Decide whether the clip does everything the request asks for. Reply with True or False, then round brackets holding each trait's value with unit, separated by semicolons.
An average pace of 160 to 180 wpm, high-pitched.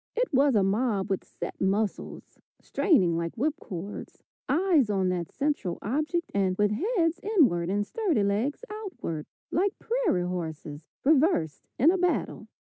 False (145 wpm; 225 Hz)